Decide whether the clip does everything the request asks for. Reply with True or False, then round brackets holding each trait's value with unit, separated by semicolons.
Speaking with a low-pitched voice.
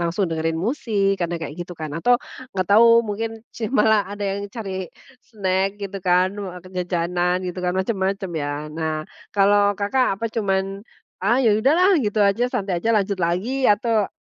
False (195 Hz)